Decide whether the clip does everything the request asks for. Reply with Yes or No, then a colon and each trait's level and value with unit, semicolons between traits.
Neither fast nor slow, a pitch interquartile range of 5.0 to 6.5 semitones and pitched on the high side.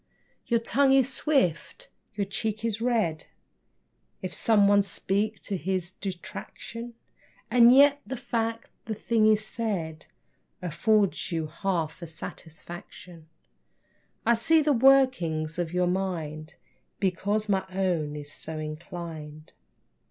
No: slow, 120 wpm; wide, 5.6 semitones; high, 195 Hz